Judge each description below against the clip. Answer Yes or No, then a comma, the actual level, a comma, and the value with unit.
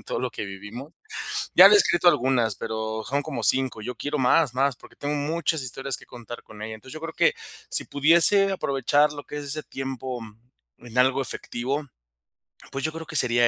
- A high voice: No, low, 135 Hz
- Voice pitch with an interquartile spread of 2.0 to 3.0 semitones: No, average, 3.7 semitones